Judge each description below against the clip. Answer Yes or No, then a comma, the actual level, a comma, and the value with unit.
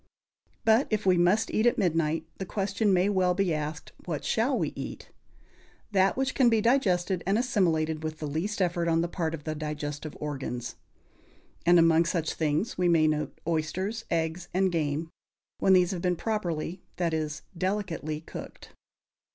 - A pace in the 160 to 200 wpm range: Yes, average, 170 wpm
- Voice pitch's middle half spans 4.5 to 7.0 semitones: No, average, 3.7 semitones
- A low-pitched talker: No, medium, 175 Hz